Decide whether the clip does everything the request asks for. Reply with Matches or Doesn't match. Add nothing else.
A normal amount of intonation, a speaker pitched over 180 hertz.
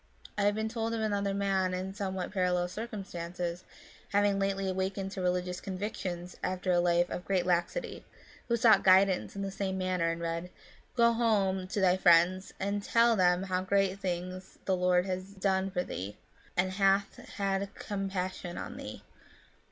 Doesn't match